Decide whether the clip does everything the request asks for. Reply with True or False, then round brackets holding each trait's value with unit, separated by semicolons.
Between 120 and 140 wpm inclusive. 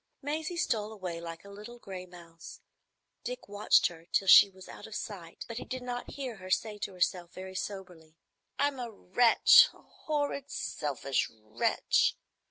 False (165 wpm)